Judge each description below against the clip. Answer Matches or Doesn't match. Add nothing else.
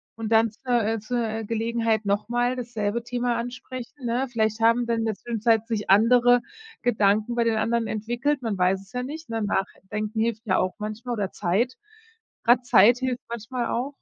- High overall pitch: Matches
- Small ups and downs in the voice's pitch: Matches